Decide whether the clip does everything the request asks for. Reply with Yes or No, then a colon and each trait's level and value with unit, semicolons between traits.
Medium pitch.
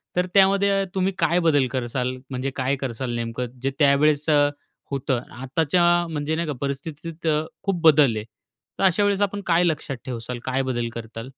Yes: medium, 145 Hz